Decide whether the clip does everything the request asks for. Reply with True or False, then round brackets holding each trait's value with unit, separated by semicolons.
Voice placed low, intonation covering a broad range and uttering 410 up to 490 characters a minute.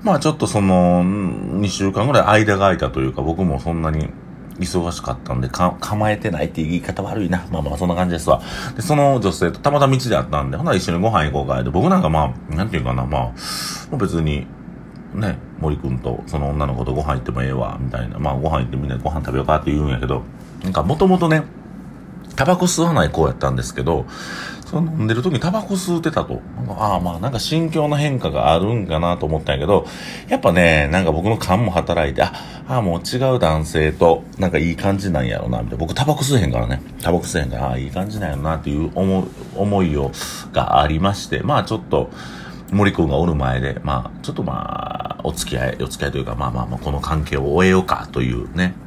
True (85 Hz; 6.7 semitones; 445 characters per minute)